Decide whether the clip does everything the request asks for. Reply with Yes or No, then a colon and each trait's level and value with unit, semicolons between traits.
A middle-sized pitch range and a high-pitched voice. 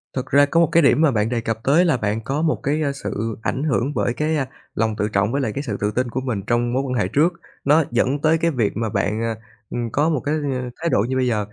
No: average, 4.6 semitones; low, 130 Hz